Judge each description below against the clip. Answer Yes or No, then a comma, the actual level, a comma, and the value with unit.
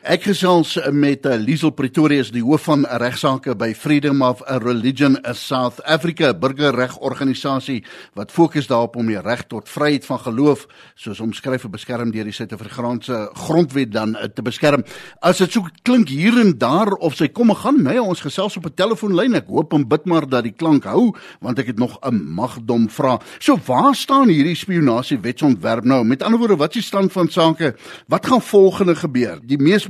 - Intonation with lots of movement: Yes, wide, 5.9 semitones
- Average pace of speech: Yes, average, 195 wpm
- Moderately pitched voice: Yes, medium, 145 Hz